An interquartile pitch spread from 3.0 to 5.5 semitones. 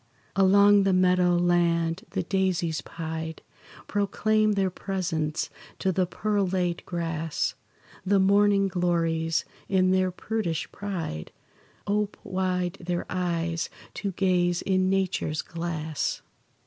No: narrow, 2.5 semitones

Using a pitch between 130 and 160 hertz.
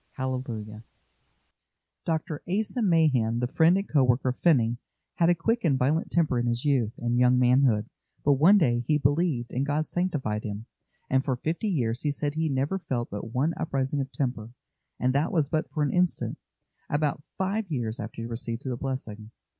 Yes: low, 135 Hz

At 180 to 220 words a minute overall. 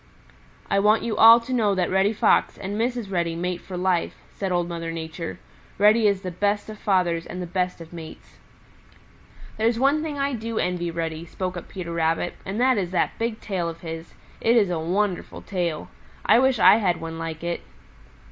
Yes: average, 200 wpm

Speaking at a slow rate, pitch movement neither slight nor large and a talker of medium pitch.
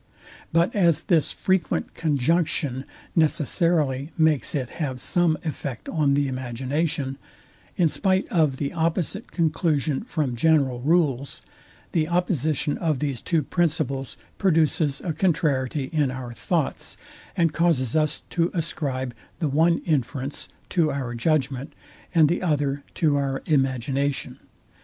Yes: slow, 125 wpm; average, 3.6 semitones; medium, 150 Hz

